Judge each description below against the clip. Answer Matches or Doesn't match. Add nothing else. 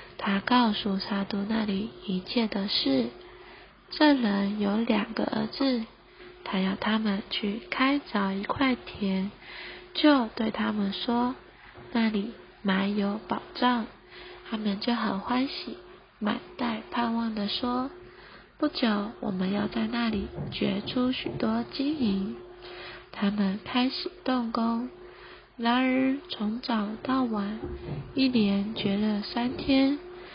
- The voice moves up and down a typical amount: Matches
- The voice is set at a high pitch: Matches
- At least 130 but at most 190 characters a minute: Matches